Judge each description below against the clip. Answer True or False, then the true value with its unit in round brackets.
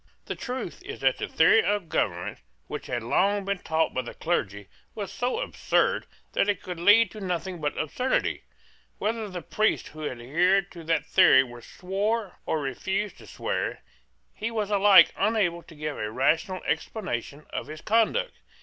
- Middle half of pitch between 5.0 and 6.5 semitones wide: True (5.4 semitones)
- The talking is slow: False (165 wpm)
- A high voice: False (180 Hz)